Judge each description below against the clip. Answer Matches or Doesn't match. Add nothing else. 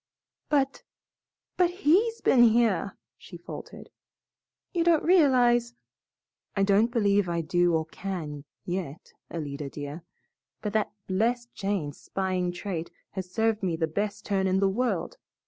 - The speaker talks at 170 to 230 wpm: Doesn't match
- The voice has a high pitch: Matches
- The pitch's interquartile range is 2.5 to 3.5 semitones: Doesn't match